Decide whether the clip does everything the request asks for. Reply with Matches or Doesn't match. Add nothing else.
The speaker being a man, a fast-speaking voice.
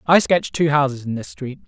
Matches